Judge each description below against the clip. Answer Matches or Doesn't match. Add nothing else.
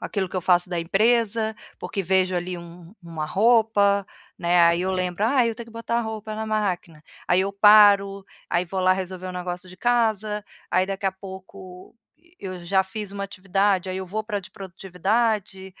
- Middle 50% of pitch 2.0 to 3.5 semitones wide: Matches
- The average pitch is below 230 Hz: Matches